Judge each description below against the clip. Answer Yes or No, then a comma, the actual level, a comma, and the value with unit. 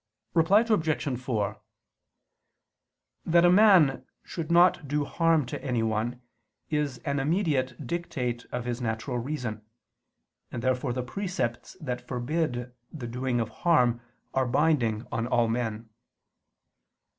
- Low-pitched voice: Yes, low, 130 Hz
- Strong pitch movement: No, average, 4.9 semitones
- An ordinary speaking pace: No, slow, 120 wpm